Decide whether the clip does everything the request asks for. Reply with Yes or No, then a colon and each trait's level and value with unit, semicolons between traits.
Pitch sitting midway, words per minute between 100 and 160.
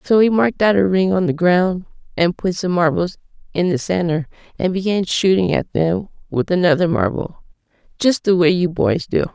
No: medium, 180 Hz; average, 185 wpm